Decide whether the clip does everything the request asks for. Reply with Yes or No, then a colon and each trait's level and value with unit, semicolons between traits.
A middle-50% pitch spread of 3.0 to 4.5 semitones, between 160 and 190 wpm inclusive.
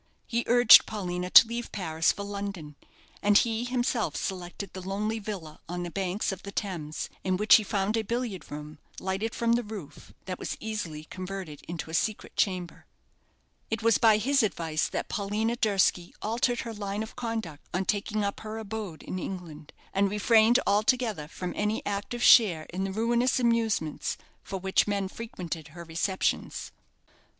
Yes: average, 3.8 semitones; average, 170 wpm